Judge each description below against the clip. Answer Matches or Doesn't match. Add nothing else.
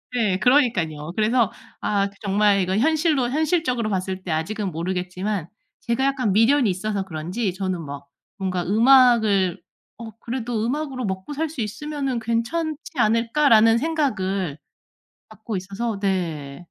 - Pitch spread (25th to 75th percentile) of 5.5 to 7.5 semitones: Doesn't match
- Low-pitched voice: Doesn't match